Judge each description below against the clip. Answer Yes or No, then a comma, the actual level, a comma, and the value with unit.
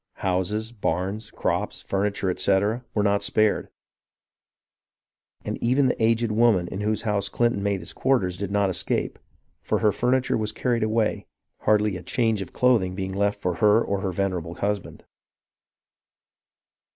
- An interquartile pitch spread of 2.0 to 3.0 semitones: Yes, average, 2.7 semitones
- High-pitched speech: No, low, 105 Hz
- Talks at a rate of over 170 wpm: No, average, 150 wpm